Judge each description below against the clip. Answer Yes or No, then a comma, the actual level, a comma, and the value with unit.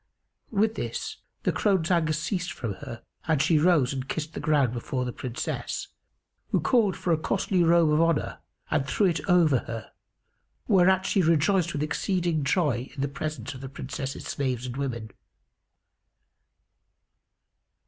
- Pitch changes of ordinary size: Yes, average, 4.9 semitones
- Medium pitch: Yes, medium, 155 Hz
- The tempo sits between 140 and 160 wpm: Yes, average, 155 wpm